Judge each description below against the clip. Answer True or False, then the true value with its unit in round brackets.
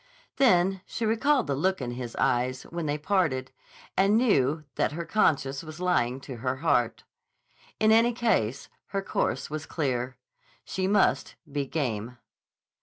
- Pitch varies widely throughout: True (7.0 semitones)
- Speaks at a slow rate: False (150 wpm)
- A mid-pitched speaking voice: True (155 Hz)